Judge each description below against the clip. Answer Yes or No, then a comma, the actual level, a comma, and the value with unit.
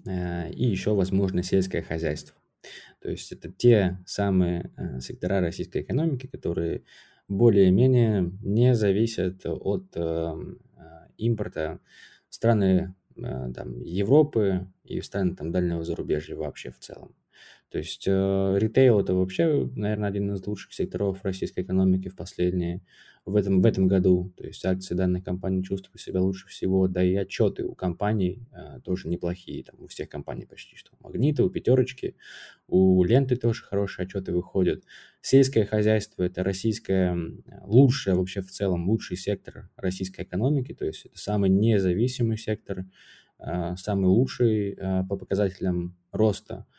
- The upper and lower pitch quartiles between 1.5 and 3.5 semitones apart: Yes, narrow, 2.6 semitones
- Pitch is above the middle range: No, very low, 95 Hz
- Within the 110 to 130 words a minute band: No, average, 140 wpm